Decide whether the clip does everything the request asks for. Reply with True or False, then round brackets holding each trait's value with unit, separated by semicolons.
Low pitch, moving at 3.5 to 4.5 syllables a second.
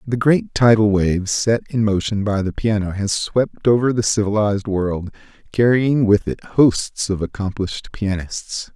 True (105 Hz; 4.3 syllables/s)